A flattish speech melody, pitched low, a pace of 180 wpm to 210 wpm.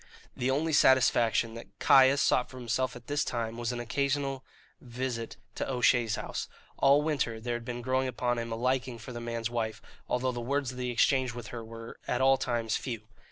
Yes: narrow, 2.1 semitones; low, 125 Hz; fast, 205 wpm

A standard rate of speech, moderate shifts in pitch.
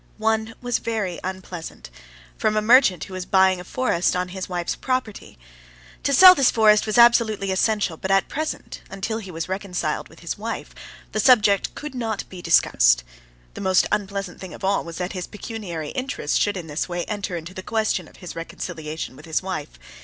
Yes: average, 190 wpm; average, 3.8 semitones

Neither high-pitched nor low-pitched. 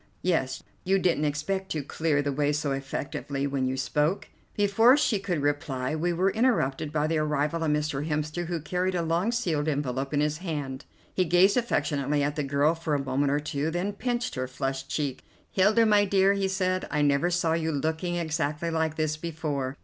Yes: medium, 155 Hz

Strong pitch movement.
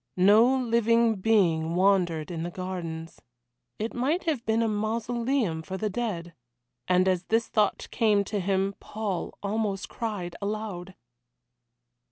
No: average, 3.8 semitones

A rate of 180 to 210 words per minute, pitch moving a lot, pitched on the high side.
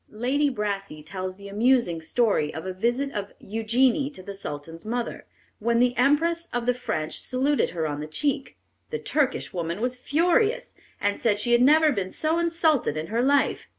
Yes: average, 185 wpm; wide, 6.3 semitones; high, 240 Hz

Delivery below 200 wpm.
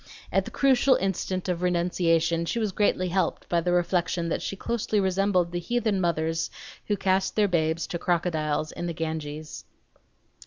Yes: average, 170 wpm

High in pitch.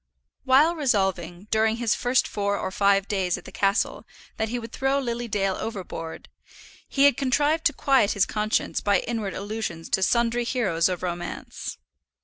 Yes: high, 215 Hz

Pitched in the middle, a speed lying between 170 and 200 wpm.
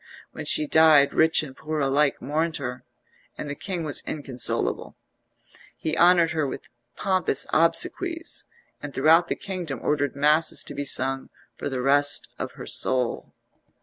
No: medium, 150 Hz; average, 150 wpm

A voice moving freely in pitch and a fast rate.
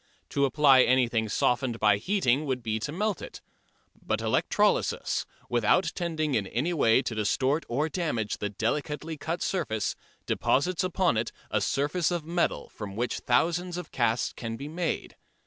No: wide, 6.3 semitones; average, 160 wpm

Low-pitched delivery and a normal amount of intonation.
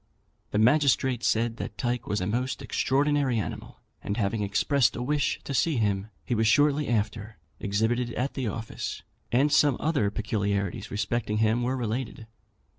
Yes: low, 120 Hz; average, 3.7 semitones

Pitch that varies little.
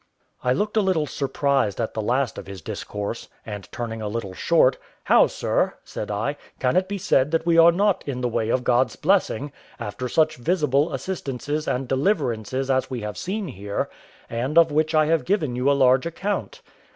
No: wide, 5.6 semitones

